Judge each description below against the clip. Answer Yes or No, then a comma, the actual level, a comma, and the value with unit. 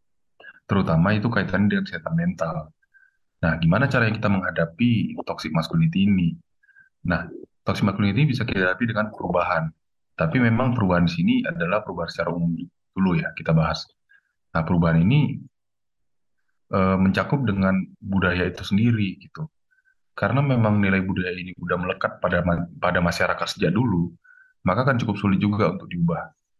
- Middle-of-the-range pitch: No, low, 100 Hz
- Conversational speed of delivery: No, fast, 145 wpm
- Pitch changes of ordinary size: No, wide, 8.3 semitones